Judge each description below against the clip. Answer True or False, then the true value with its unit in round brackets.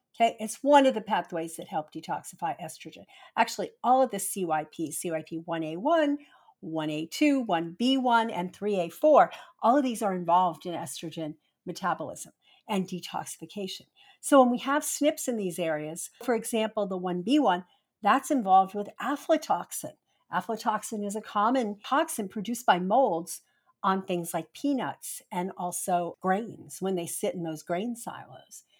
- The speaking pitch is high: True (195 Hz)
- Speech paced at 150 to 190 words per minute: False (140 wpm)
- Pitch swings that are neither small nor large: False (6.8 semitones)